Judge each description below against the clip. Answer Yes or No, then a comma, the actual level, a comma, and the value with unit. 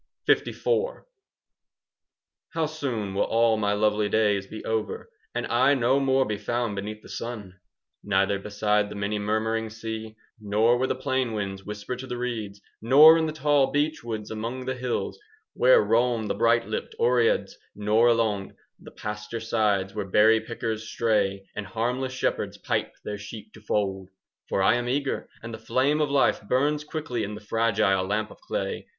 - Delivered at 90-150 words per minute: No, average, 175 wpm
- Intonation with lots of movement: No, average, 3.2 semitones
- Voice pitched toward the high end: No, low, 110 Hz